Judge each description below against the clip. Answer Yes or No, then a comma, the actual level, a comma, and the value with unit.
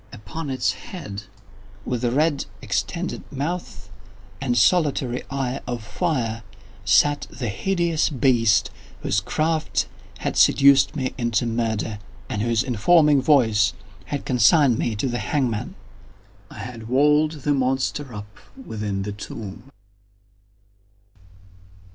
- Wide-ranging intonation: No, average, 4.9 semitones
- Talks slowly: Yes, slow, 115 wpm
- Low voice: Yes, low, 125 Hz